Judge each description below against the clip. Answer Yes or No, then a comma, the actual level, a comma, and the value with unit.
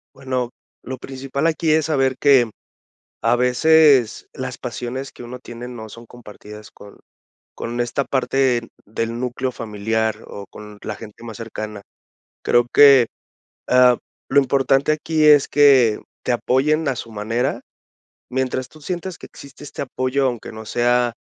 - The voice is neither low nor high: No, low, 125 Hz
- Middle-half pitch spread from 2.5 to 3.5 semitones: Yes, average, 2.9 semitones